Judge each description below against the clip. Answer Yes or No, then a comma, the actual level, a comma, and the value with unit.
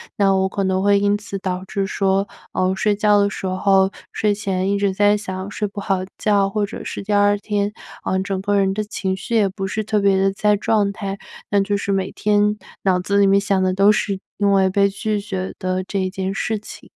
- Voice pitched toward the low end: No, high, 200 Hz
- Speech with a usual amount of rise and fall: No, narrow, 1.2 semitones